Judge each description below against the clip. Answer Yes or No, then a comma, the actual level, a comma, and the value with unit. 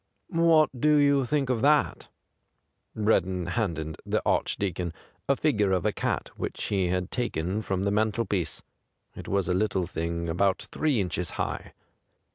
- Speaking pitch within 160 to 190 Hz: No, low, 100 Hz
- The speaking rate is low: No, average, 160 wpm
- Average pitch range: No, wide, 5.9 semitones